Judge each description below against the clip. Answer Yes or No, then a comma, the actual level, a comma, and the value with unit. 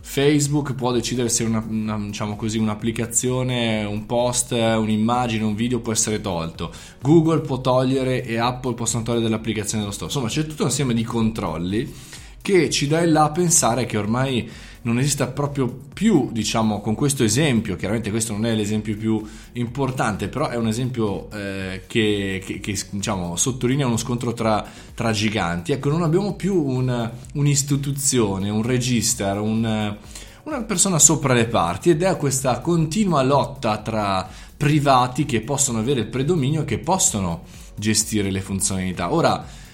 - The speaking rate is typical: Yes, average, 160 wpm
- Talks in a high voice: No, low, 115 Hz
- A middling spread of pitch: Yes, average, 3.8 semitones